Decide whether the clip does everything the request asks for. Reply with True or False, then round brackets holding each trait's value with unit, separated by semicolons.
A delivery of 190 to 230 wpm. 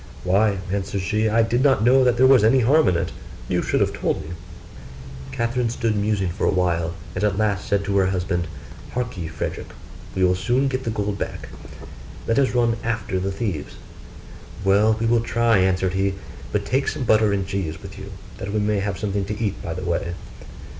True (205 wpm)